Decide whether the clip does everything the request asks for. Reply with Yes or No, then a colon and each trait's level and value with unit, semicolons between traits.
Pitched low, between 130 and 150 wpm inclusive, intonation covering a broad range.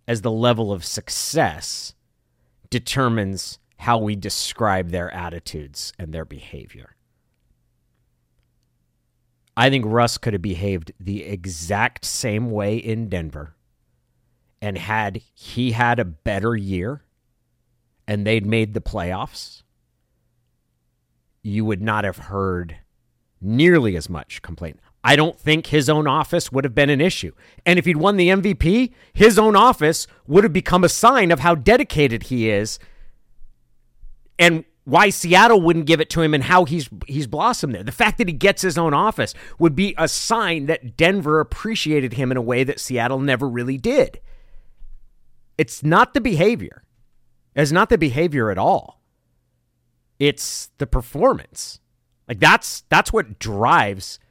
Yes: low, 120 Hz; average, 145 wpm; wide, 8.6 semitones